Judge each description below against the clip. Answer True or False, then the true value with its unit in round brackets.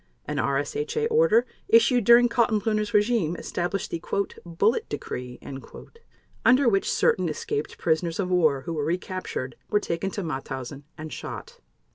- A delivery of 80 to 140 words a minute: True (135 wpm)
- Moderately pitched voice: True (180 Hz)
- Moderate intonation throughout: False (6.9 semitones)